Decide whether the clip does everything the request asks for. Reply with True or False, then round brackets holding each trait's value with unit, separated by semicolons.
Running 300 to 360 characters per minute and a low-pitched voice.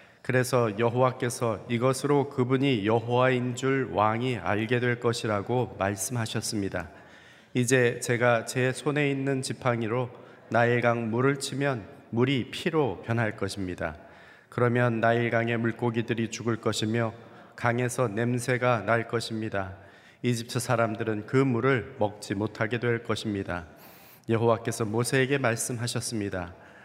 False (290 characters per minute; 120 Hz)